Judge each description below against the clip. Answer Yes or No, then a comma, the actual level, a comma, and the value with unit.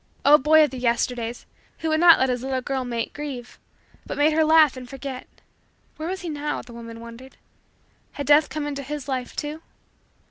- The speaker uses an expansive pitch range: No, average, 3.4 semitones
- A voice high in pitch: Yes, very high, 275 Hz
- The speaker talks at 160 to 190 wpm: No, average, 200 wpm